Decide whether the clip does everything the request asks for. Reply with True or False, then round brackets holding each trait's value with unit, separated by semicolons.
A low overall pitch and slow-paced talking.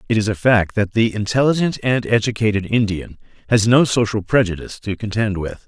False (110 Hz; 180 wpm)